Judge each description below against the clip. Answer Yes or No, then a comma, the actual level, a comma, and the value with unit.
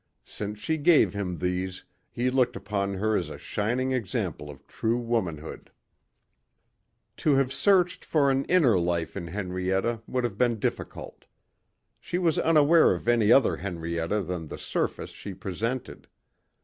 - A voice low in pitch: Yes, low, 110 Hz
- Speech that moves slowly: No, average, 150 wpm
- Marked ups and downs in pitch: Yes, wide, 6.0 semitones